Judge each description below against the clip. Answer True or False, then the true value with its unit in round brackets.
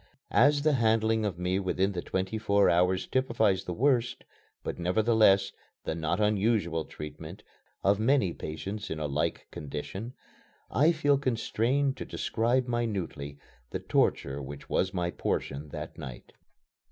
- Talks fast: False (140 wpm)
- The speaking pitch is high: False (100 Hz)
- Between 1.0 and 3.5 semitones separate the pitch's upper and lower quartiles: False (5.2 semitones)